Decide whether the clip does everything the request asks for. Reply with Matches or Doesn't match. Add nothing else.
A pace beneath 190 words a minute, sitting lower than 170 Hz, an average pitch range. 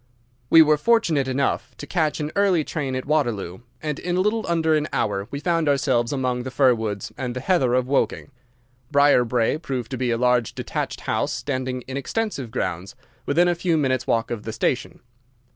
Doesn't match